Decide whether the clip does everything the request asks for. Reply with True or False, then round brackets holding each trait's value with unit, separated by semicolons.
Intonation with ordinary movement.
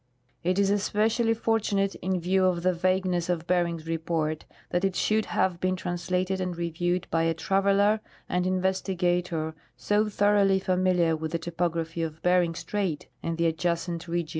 False (2.3 semitones)